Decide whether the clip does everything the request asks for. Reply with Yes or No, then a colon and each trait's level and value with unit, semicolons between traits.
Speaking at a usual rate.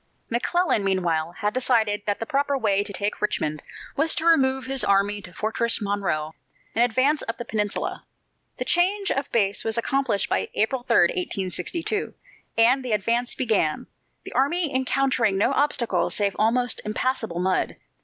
Yes: average, 155 wpm